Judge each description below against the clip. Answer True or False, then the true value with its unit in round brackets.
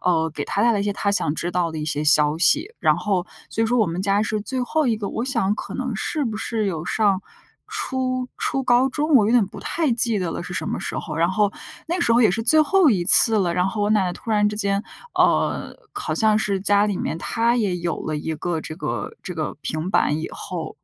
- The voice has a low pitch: False (205 Hz)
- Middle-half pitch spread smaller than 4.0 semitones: False (5.1 semitones)